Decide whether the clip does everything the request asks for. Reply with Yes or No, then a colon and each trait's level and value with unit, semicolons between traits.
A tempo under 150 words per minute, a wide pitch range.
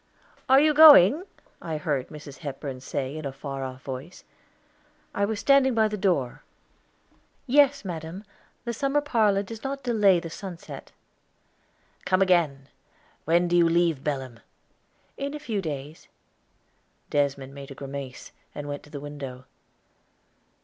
Yes: average, 140 wpm; wide, 7.6 semitones